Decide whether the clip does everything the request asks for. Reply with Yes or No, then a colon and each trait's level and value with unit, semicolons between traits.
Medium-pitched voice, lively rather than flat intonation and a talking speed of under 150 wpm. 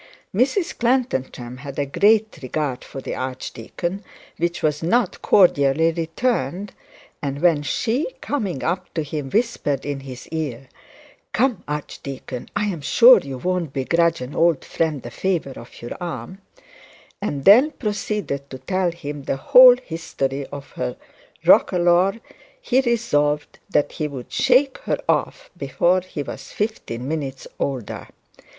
Yes: medium, 160 Hz; wide, 6.9 semitones; average, 140 wpm